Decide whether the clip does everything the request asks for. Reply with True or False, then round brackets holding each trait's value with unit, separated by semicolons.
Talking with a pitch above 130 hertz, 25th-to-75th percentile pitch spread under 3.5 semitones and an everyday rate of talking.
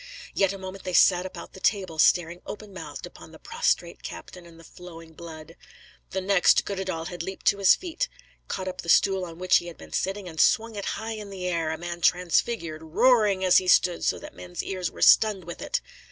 False (185 Hz; 2.5 semitones; 215 wpm)